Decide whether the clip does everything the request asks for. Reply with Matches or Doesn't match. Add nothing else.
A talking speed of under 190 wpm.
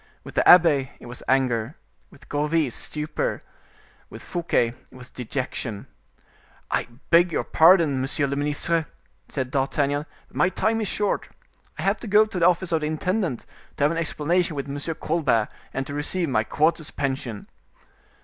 Matches